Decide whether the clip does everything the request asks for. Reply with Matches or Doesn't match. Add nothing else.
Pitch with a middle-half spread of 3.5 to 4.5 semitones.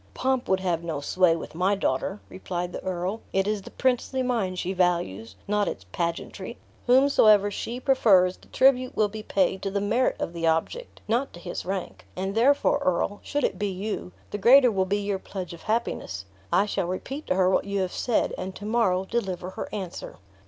Matches